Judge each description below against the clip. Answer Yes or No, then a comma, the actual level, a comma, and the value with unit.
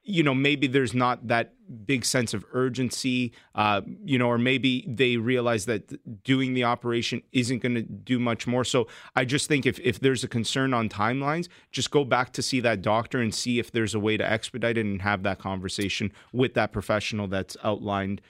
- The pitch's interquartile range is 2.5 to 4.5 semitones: Yes, average, 3.2 semitones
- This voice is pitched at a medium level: No, low, 120 Hz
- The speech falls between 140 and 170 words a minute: No, fast, 205 wpm